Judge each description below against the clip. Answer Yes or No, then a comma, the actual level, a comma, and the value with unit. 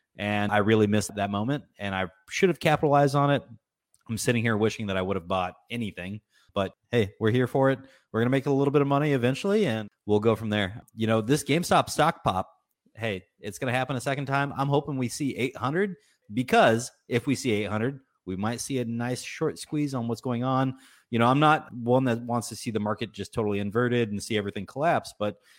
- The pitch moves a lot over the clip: No, average, 4.4 semitones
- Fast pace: Yes, fast, 230 wpm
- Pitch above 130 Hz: No, low, 120 Hz